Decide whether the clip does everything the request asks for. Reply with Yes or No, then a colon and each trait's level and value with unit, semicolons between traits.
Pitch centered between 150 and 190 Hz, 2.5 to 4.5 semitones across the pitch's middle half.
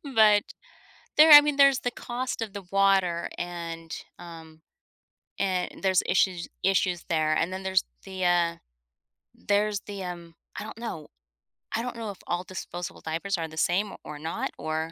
Yes: medium, 185 Hz; average, 3.4 semitones